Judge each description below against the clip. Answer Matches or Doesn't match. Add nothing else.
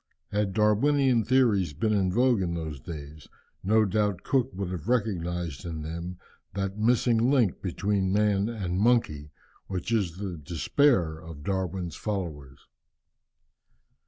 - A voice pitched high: Doesn't match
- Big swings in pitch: Doesn't match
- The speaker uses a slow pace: Matches